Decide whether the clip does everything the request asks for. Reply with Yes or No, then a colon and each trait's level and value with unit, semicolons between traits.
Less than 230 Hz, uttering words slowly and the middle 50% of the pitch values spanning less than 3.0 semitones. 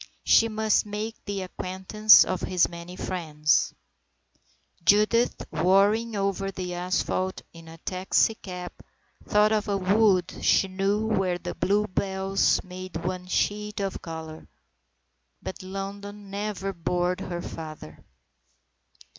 Yes: high, 190 Hz; slow, 120 wpm; narrow, 2.4 semitones